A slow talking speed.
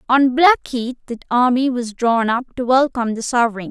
No: average, 180 wpm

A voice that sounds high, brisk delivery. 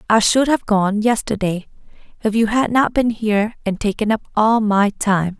No: high, 215 Hz; average, 190 wpm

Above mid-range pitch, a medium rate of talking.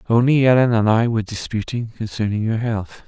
No: low, 110 Hz; average, 175 wpm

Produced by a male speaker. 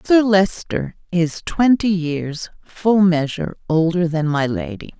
No: female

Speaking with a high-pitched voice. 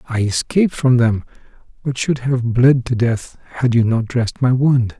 No: low, 125 Hz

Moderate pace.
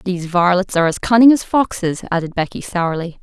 Yes: average, 185 wpm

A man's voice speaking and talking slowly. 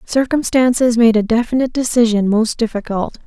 No: female; slow, 130 wpm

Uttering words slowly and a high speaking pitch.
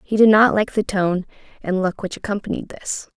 No: fast, 205 wpm; high, 200 Hz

